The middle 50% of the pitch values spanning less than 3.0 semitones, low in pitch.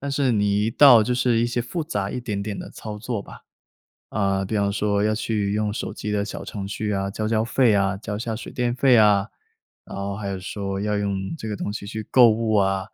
Yes: narrow, 2.5 semitones; low, 105 Hz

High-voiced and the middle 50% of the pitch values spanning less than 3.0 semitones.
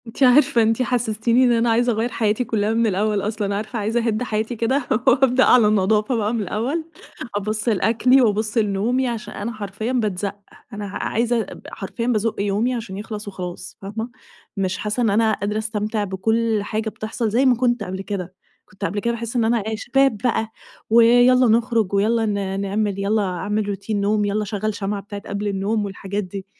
Yes: high, 215 Hz; narrow, 2.4 semitones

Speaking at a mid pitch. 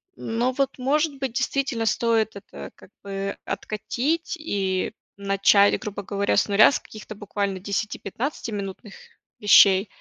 No: high, 215 Hz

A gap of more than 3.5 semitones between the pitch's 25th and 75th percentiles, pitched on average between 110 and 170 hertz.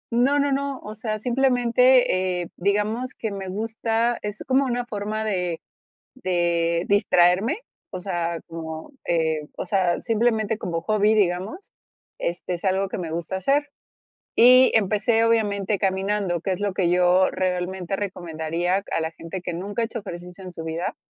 No: average, 4.1 semitones; high, 195 Hz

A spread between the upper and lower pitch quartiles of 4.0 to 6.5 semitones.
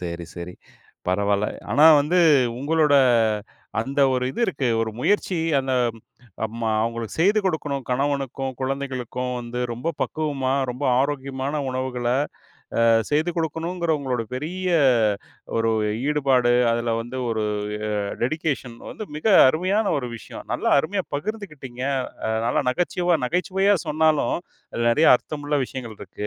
Yes: average, 4.6 semitones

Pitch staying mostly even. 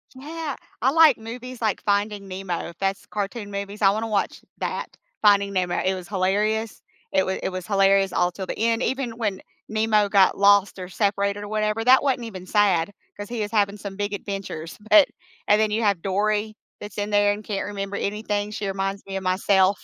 Yes: narrow, 1.8 semitones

